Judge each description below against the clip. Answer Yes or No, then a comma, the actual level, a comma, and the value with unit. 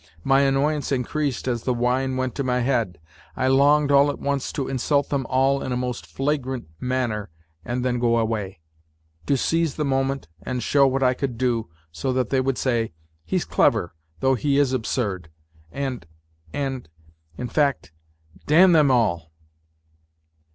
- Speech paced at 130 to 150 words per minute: No, average, 165 wpm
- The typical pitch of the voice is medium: No, low, 130 Hz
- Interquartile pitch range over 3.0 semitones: No, narrow, 2.5 semitones